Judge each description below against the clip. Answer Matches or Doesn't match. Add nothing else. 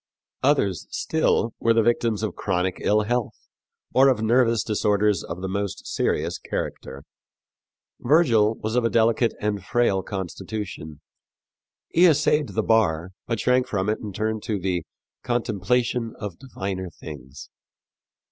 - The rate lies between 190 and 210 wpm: Doesn't match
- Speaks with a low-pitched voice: Matches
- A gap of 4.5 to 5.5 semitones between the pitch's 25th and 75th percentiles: Doesn't match